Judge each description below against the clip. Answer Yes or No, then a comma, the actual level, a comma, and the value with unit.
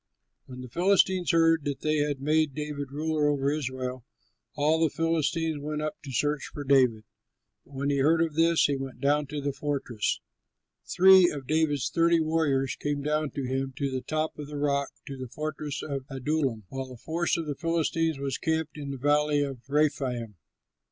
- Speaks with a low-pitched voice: No, medium, 145 Hz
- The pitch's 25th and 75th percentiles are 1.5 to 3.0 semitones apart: Yes, narrow, 2.5 semitones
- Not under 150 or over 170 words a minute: No, average, 190 wpm